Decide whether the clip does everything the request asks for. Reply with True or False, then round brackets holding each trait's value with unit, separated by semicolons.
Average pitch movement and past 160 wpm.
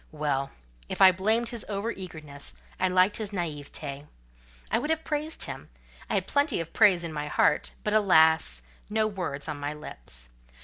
False (6.2 semitones; 175 wpm)